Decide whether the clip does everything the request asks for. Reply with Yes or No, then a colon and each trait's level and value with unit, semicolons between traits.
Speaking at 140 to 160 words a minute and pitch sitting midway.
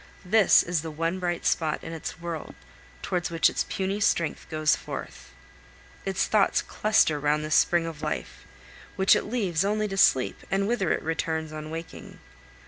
No: average, 170 wpm; medium, 165 Hz